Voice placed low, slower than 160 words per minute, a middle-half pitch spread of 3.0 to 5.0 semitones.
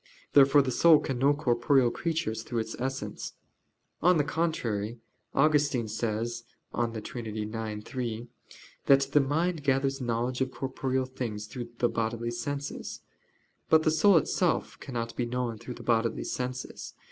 Yes: low, 125 Hz; average, 145 wpm; average, 3.3 semitones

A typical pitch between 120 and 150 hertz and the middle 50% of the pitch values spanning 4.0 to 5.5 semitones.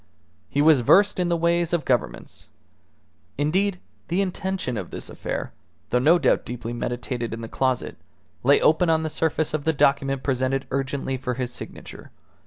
Yes: medium, 140 Hz; average, 5.1 semitones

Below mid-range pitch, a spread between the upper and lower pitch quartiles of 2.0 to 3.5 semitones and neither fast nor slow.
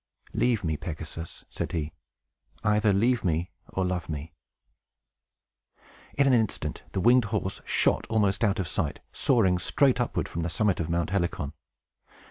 No: very low, 95 Hz; average, 5.0 semitones; average, 150 wpm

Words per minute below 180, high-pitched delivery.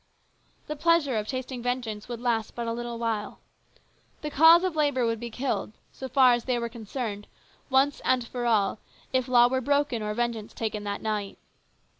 No: average, 185 wpm; high, 240 Hz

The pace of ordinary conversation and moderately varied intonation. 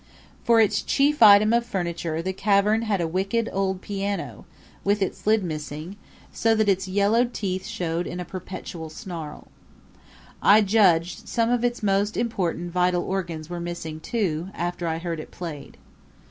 Yes: average, 160 wpm; average, 3.7 semitones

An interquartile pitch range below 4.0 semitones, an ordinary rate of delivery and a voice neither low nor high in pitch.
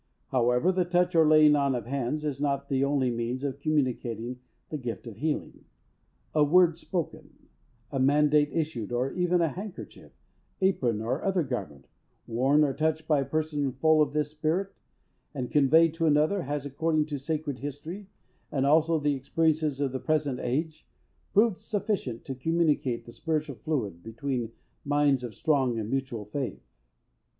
Yes: average, 3.5 semitones; average, 160 wpm; medium, 145 Hz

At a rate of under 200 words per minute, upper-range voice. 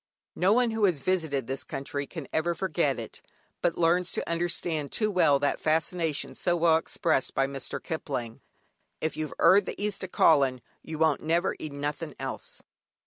No: average, 175 wpm; medium, 160 Hz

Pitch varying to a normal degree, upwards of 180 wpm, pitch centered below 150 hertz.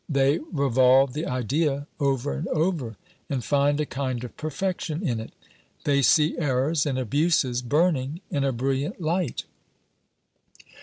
No: average, 3.2 semitones; average, 140 wpm; medium, 140 Hz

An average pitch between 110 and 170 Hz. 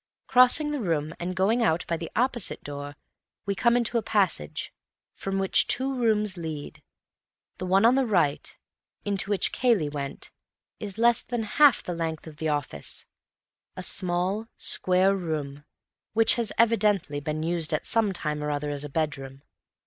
No: medium, 185 Hz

